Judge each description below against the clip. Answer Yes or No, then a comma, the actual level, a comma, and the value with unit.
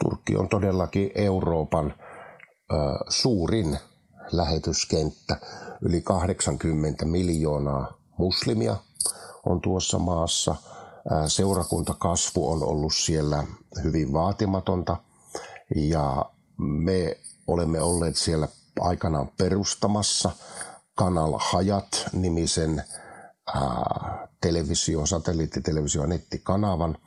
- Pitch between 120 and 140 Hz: No, very low, 85 Hz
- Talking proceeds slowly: Yes, slow, 70 wpm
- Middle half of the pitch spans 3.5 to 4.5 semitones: No, average, 3.1 semitones